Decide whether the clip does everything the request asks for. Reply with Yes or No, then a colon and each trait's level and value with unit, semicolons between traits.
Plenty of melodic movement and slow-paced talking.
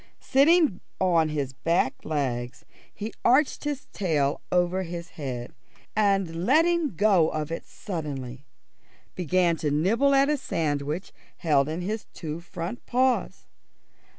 Yes: wide, 6.3 semitones; slow, 125 wpm